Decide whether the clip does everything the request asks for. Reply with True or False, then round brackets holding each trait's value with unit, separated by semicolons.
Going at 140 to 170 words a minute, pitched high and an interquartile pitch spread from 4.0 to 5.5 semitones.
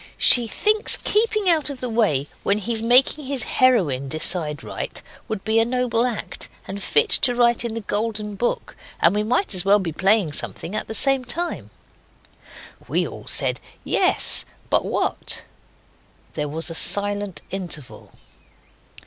True (155 wpm; 220 Hz; 4.7 semitones)